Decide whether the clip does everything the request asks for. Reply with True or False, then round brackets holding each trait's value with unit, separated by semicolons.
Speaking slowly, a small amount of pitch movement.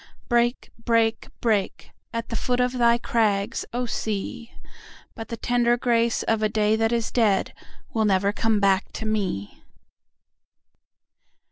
True (125 wpm; 2.1 semitones)